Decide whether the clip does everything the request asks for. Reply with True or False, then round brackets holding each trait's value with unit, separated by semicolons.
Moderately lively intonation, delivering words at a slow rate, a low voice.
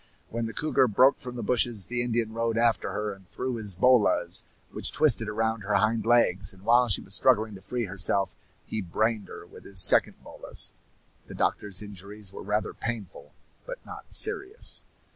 False (3.0 semitones; 180 wpm; 110 Hz)